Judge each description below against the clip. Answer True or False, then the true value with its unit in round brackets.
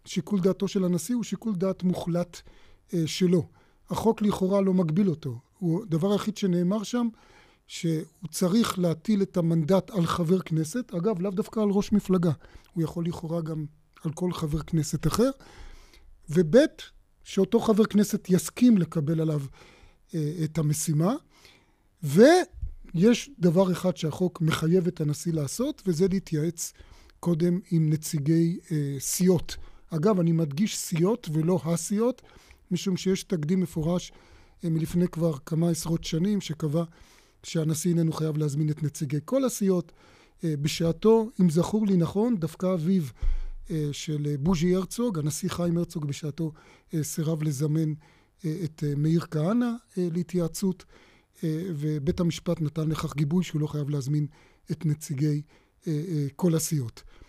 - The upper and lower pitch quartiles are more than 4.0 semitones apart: False (3.3 semitones)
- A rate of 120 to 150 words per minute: True (130 wpm)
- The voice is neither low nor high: True (170 Hz)